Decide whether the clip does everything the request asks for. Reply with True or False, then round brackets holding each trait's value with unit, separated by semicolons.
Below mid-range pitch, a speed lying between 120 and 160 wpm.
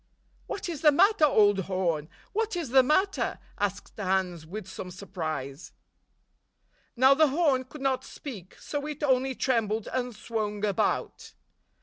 False (240 Hz; 140 wpm)